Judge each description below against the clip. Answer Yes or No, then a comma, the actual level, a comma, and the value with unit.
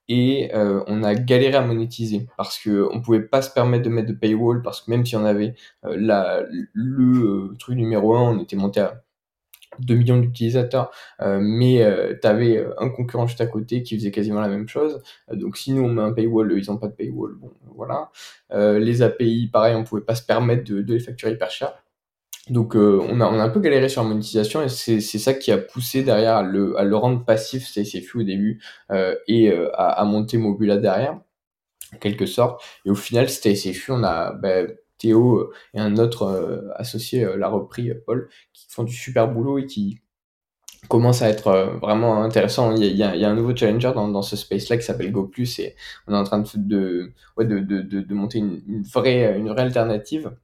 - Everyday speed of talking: No, fast, 225 wpm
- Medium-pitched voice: No, low, 110 Hz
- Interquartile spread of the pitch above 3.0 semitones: No, average, 2.7 semitones